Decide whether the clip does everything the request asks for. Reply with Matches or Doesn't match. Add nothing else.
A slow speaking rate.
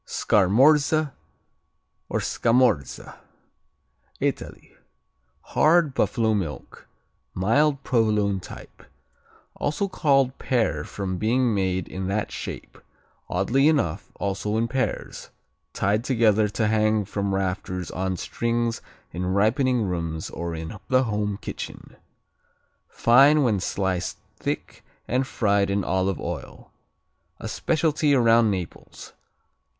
Matches